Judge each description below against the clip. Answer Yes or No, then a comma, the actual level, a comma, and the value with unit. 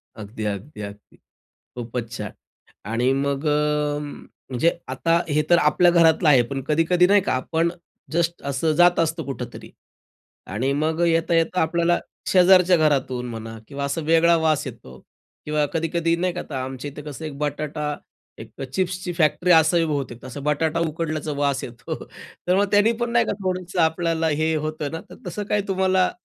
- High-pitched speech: No, medium, 155 Hz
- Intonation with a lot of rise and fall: No, average, 3.8 semitones